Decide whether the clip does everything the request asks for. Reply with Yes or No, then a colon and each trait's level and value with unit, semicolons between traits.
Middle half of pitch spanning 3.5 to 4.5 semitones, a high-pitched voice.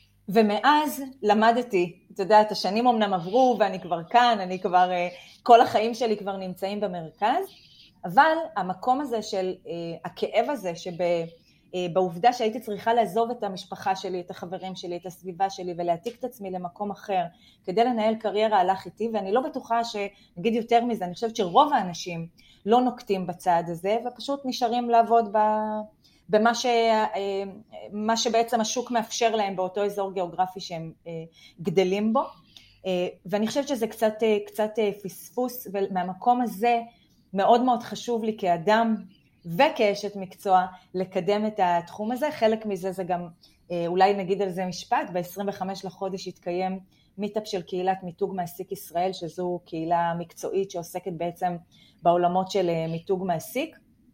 Yes: average, 3.9 semitones; high, 200 Hz